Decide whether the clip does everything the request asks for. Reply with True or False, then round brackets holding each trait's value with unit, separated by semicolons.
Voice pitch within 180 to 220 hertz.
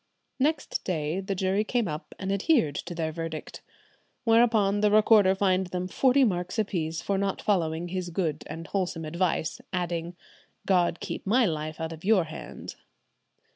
True (185 Hz)